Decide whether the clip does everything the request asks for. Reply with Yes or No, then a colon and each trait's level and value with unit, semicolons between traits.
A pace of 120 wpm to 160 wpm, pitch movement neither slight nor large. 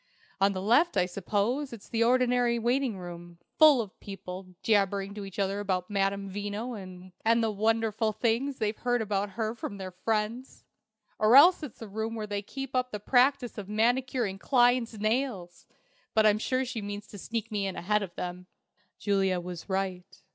No: average, 180 wpm; average, 3.5 semitones